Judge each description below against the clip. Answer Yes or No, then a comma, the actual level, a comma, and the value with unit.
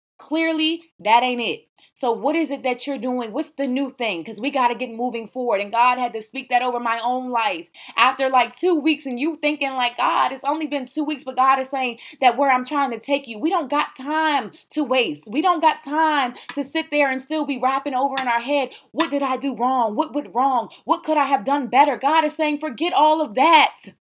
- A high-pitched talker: Yes, very high, 275 Hz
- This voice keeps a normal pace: No, fast, 245 wpm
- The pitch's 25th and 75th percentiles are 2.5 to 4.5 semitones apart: Yes, average, 3.3 semitones